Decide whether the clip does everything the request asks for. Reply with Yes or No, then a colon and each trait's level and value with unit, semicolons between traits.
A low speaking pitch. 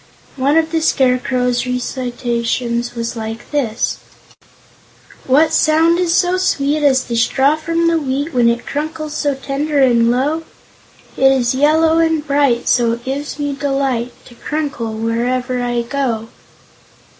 No: very high, 270 Hz